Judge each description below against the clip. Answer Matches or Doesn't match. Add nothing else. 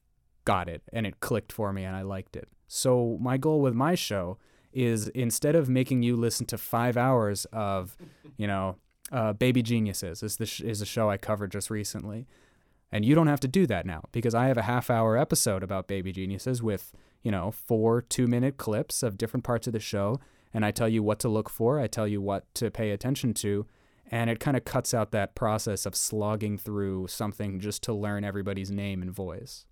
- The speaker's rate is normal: Doesn't match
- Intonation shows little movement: Doesn't match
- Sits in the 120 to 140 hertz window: Doesn't match